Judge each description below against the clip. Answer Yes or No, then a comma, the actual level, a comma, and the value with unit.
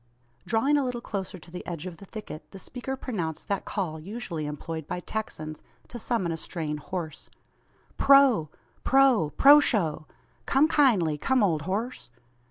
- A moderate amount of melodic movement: No, wide, 7.3 semitones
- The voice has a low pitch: No, high, 190 Hz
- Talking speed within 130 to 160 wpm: Yes, average, 155 wpm